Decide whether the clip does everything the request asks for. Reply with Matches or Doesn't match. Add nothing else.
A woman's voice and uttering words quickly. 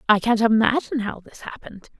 Doesn't match